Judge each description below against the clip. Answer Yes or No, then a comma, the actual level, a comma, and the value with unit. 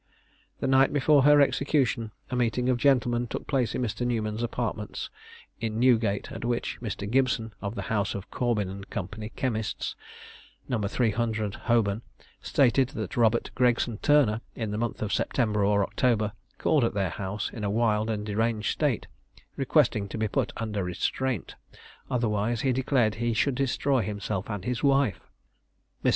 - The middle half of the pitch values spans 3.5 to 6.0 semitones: No, average, 3.0 semitones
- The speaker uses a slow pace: No, average, 160 wpm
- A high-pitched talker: No, low, 115 Hz